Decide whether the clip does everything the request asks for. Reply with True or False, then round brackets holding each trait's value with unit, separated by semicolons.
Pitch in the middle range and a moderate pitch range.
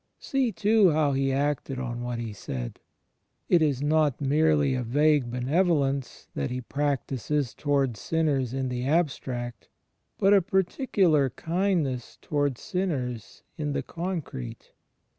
True (145 Hz; 4.3 semitones)